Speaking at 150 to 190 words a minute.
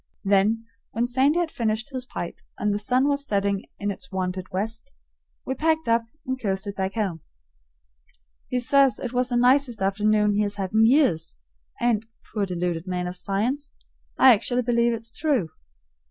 Yes: average, 170 wpm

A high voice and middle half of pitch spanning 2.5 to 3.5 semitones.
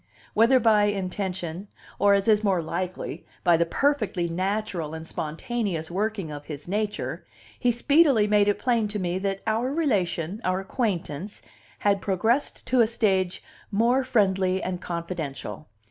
No: high, 195 Hz; average, 3.9 semitones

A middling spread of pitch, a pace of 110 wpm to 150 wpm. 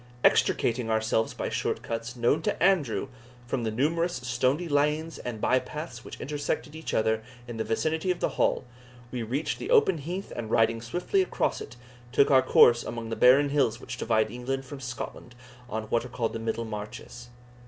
No: average, 4.5 semitones; average, 185 wpm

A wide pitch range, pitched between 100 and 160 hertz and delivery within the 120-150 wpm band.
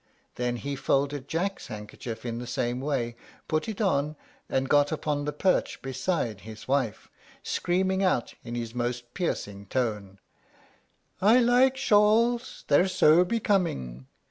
Yes: wide, 7.7 semitones; medium, 140 Hz; average, 140 wpm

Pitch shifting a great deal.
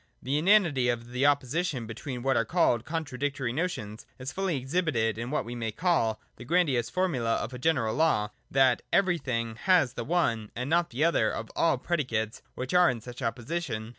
Yes: wide, 5.9 semitones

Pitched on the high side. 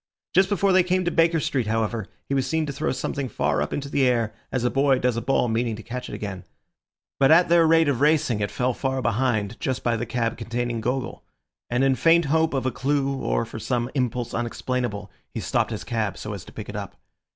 No: low, 125 Hz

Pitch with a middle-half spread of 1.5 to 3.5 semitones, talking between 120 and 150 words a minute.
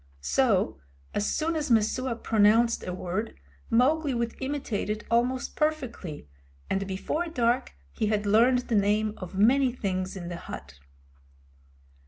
No: average, 4.6 semitones; average, 140 wpm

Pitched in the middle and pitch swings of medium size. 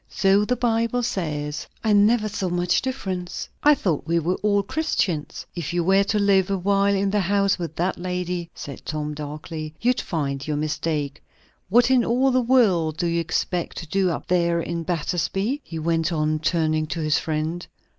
Yes: medium, 175 Hz; average, 4.3 semitones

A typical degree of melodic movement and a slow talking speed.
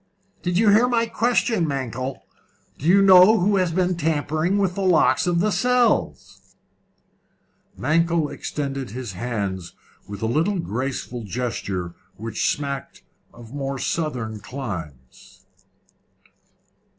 No: wide, 7.8 semitones; slow, 120 wpm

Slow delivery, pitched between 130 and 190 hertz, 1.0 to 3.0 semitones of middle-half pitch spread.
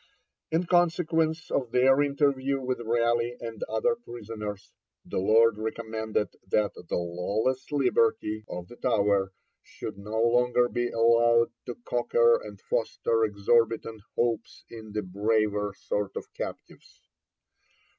No: slow, 125 wpm; low, 115 Hz; narrow, 2.6 semitones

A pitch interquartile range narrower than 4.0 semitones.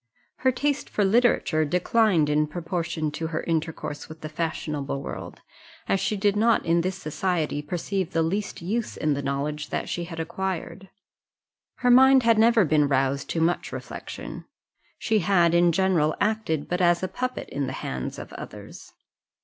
No: average, 4.7 semitones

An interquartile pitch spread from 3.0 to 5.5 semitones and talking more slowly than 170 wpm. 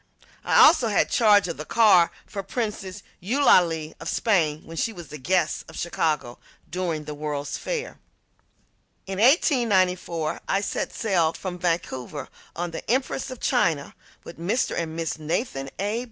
Yes: average, 5.1 semitones; average, 155 wpm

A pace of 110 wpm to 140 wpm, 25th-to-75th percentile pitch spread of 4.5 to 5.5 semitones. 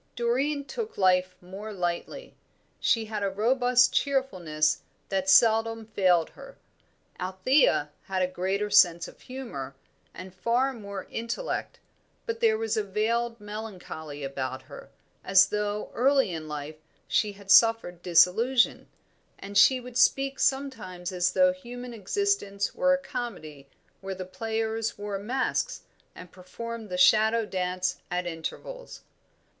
Yes: slow, 135 wpm; average, 5.1 semitones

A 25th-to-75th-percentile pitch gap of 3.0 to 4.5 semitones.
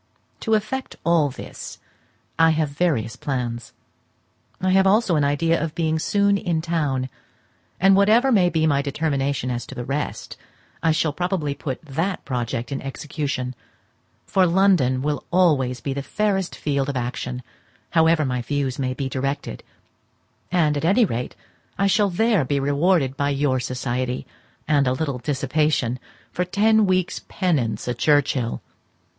No: average, 5.3 semitones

